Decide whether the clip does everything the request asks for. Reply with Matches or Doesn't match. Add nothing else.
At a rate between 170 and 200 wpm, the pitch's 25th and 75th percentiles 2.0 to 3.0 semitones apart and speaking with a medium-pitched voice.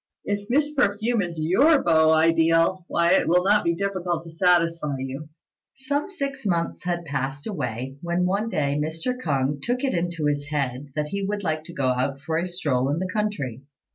Doesn't match